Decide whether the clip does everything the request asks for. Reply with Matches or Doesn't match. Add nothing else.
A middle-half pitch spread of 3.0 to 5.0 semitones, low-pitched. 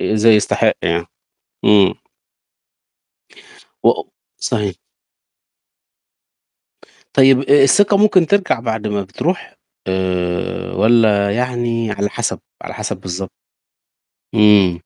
Matches